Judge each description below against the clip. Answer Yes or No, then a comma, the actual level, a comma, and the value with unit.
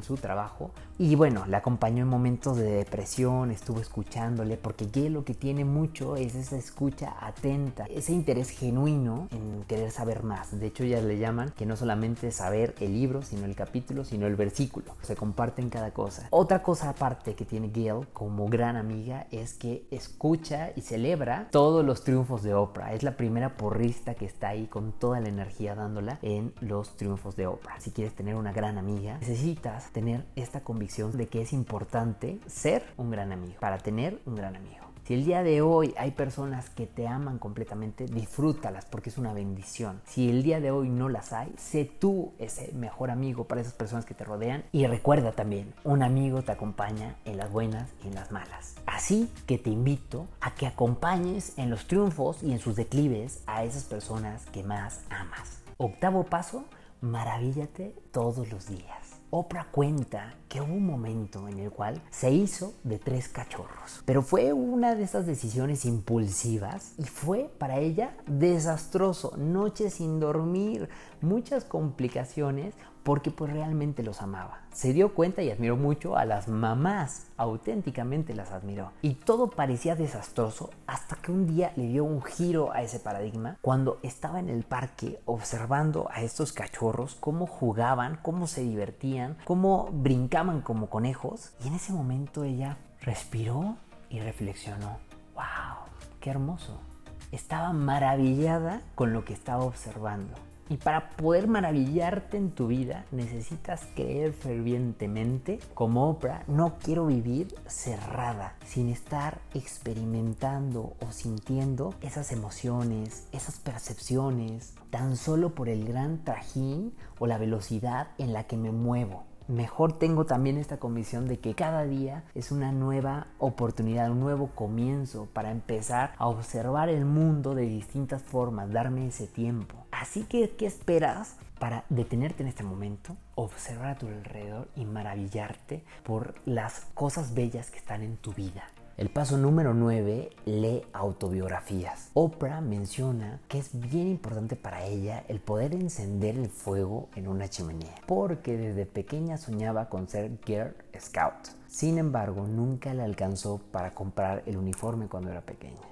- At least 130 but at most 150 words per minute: No, average, 160 wpm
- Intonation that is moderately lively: Yes, average, 4.8 semitones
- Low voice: Yes, low, 120 Hz